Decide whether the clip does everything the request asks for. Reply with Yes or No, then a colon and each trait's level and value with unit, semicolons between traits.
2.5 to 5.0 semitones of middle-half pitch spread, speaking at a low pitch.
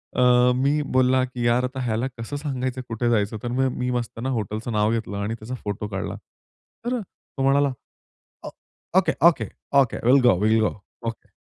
Yes: average, 2.8 semitones; low, 125 Hz